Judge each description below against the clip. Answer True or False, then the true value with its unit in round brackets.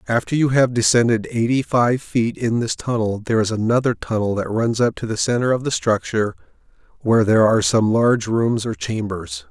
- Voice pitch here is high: False (115 Hz)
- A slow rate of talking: False (195 wpm)